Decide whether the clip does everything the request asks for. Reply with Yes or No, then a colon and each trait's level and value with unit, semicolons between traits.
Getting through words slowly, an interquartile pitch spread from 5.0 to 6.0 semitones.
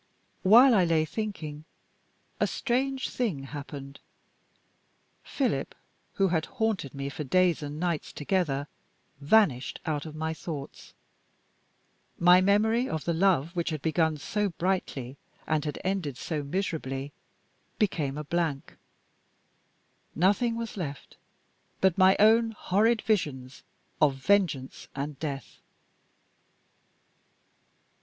Yes: slow, 115 wpm; wide, 5.5 semitones